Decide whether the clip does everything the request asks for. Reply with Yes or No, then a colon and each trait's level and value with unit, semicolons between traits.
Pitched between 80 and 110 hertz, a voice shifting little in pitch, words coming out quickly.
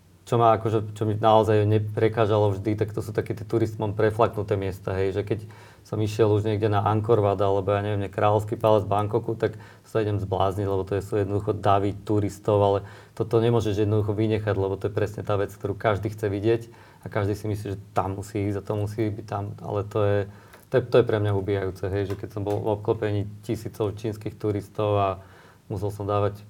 Yes: low, 105 Hz; narrow, 1.4 semitones; fast, 220 wpm